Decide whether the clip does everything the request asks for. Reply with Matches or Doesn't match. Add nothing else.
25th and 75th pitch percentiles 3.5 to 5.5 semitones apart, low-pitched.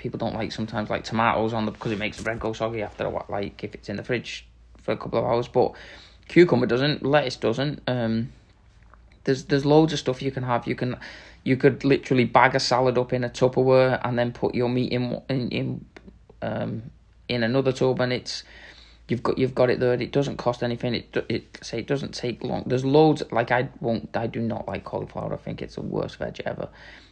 Doesn't match